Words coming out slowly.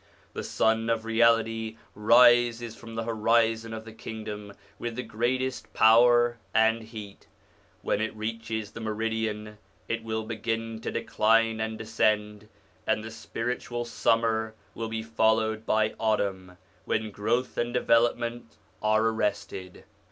Yes: slow, 130 wpm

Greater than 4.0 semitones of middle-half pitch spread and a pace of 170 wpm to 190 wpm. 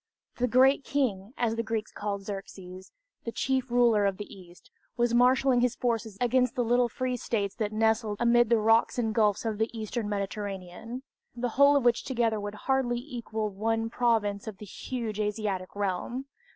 No: average, 2.9 semitones; average, 180 wpm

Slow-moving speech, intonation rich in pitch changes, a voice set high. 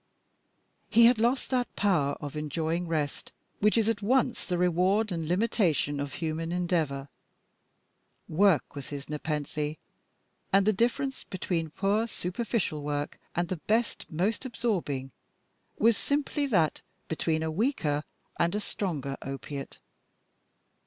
No: slow, 130 wpm; wide, 6.2 semitones; medium, 175 Hz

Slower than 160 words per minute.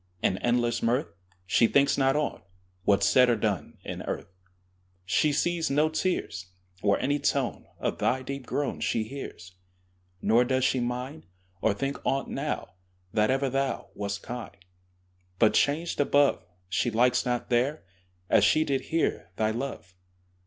Yes: average, 150 wpm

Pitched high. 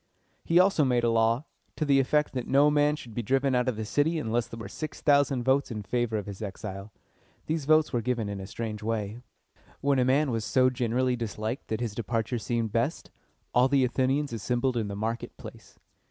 No: low, 120 Hz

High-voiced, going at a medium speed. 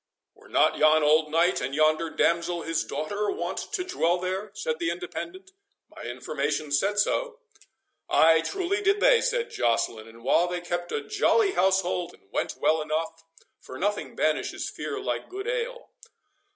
No: medium, 180 Hz; average, 165 wpm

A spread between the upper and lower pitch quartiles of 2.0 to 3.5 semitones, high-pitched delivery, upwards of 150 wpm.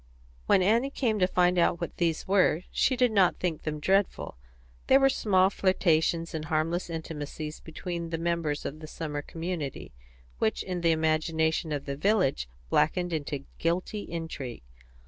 No: average, 3.0 semitones; medium, 165 Hz; average, 160 wpm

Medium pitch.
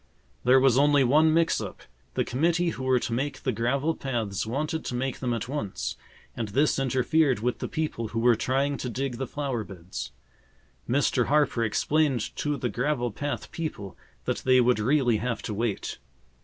No: low, 130 Hz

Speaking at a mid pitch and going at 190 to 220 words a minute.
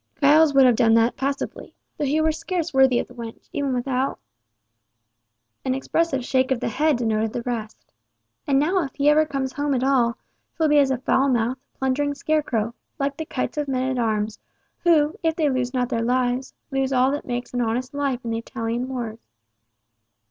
No: very high, 265 Hz; average, 200 wpm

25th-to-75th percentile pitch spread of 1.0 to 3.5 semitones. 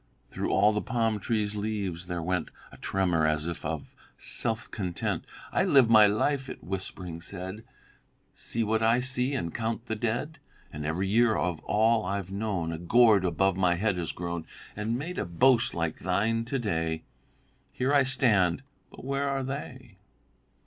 No: average, 4.9 semitones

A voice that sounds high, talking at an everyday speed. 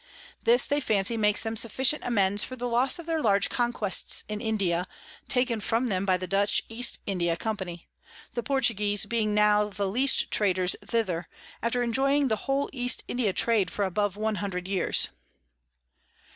Yes: high, 215 Hz; average, 165 wpm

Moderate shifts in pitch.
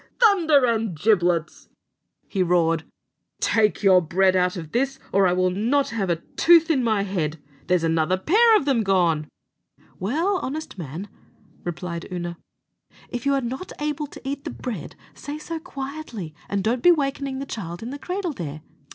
No: wide, 8.0 semitones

